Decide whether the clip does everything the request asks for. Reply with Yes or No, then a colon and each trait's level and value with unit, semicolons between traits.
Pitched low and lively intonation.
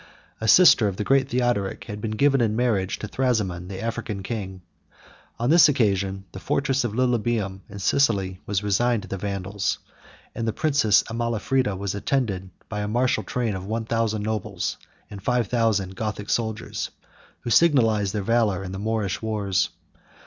No: low, 110 Hz; average, 3.4 semitones